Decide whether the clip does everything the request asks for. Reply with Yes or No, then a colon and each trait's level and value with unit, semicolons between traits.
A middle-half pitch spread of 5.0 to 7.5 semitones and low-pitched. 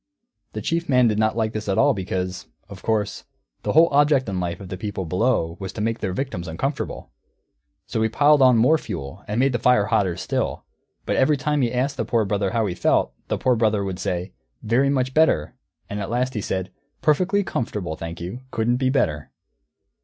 Yes: wide, 5.5 semitones; low, 110 Hz